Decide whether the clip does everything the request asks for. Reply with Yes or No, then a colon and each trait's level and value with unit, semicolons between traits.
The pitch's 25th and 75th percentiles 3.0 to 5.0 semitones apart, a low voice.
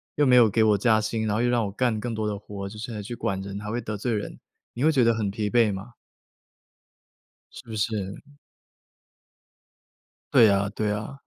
No: narrow, 2.4 semitones; low, 110 Hz